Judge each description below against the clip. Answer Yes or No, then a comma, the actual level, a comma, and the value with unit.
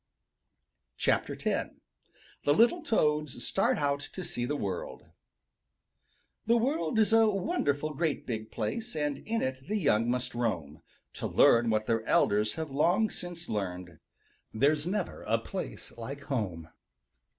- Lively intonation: Yes, wide, 8.4 semitones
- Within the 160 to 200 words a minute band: No, average, 140 wpm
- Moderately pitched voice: Yes, medium, 145 Hz